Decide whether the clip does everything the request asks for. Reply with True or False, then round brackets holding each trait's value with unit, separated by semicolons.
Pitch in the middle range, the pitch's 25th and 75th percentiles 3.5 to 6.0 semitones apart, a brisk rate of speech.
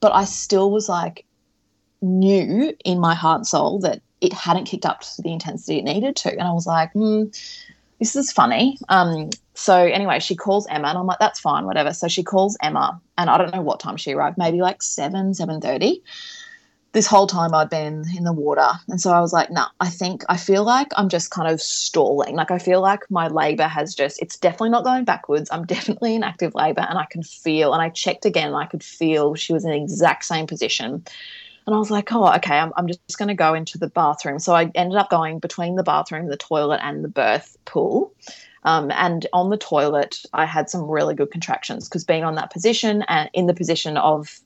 True (180 Hz; 4.0 semitones; 230 wpm)